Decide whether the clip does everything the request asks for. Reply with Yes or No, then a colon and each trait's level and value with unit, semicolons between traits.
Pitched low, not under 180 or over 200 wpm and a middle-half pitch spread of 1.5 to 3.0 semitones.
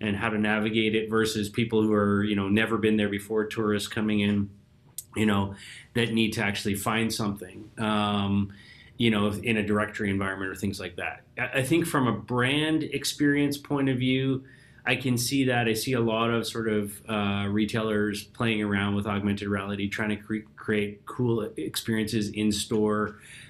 Yes: low, 110 Hz; average, 185 wpm; narrow, 2.5 semitones